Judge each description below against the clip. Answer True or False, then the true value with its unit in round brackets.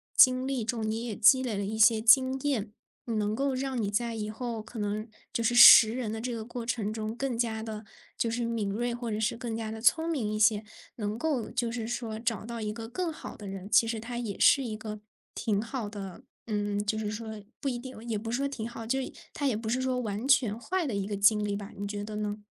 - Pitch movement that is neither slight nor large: False (2.3 semitones)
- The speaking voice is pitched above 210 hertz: True (225 Hz)